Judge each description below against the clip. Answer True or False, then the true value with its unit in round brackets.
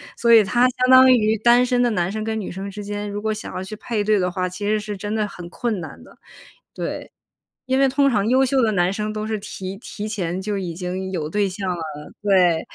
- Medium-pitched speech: False (210 Hz)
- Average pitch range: True (3.2 semitones)